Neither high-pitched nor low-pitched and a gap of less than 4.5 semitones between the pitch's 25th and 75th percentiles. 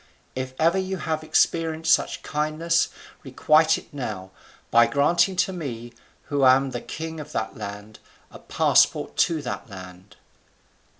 No: medium, 145 Hz; wide, 5.5 semitones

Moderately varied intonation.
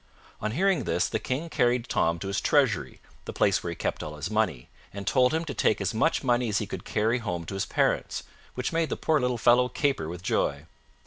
Yes: average, 4.8 semitones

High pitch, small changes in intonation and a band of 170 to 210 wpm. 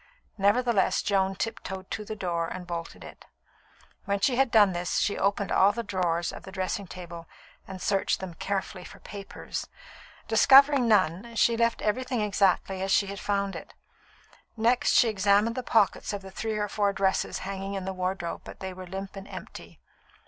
Yes: high, 195 Hz; narrow, 2.2 semitones; average, 180 wpm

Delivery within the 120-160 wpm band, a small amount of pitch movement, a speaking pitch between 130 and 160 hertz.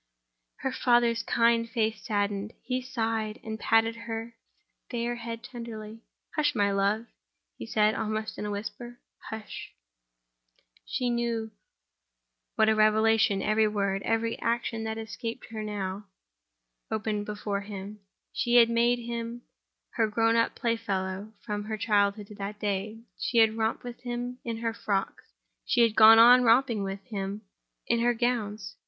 No: average, 150 wpm; narrow, 1.8 semitones; high, 225 Hz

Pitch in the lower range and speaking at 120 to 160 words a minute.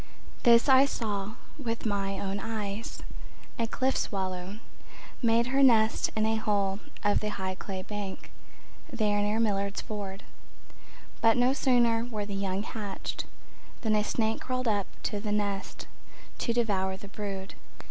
No: high, 210 Hz; average, 145 wpm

